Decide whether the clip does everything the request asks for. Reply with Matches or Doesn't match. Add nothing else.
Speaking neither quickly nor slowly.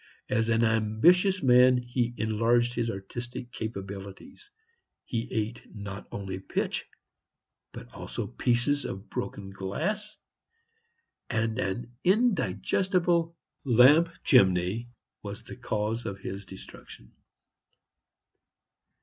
Doesn't match